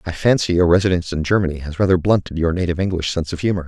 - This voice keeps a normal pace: No, fast, 245 wpm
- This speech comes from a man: Yes, male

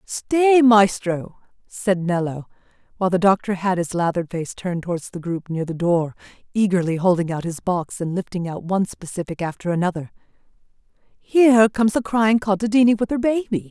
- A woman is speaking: Yes, female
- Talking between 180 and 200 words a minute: No, average, 165 wpm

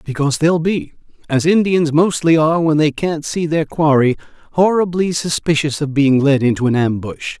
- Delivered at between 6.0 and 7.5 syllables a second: No, 5.1 syllables/s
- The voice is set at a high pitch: No, medium, 155 Hz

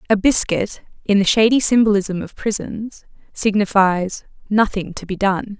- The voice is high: Yes, high, 205 Hz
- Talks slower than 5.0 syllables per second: Yes, 4.5 syllables/s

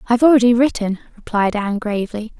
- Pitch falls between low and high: No, high, 225 Hz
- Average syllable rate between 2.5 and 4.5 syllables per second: No, 6.8 syllables/s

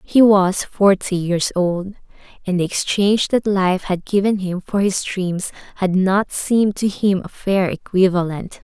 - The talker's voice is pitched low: No, high, 190 Hz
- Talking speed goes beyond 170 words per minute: No, average, 165 wpm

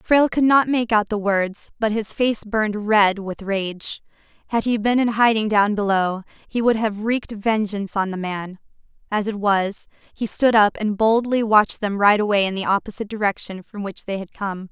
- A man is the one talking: No, female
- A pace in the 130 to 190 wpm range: No, fast, 205 wpm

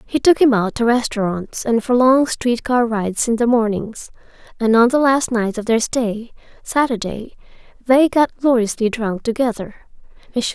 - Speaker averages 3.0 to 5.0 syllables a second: Yes, 4.5 syllables/s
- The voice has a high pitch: Yes, high, 235 Hz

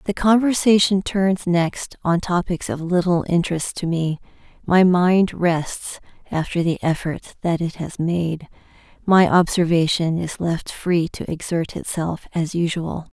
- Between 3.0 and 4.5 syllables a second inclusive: Yes, 4.0 syllables/s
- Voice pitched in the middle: Yes, medium, 175 Hz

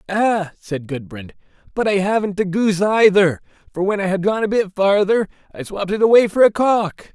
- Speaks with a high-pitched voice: Yes, high, 195 Hz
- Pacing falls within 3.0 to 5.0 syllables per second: No, 5.2 syllables/s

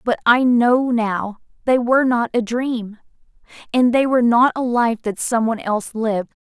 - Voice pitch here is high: Yes, high, 235 Hz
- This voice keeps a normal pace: Yes, average, 185 wpm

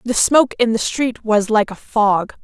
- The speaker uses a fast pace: Yes, fast, 220 wpm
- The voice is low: No, high, 225 Hz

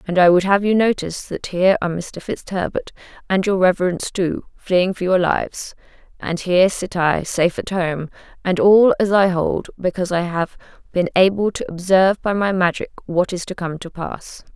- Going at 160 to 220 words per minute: Yes, average, 195 wpm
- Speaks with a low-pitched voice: No, medium, 185 Hz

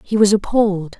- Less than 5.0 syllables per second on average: No, 5.6 syllables/s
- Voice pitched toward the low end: No, high, 200 Hz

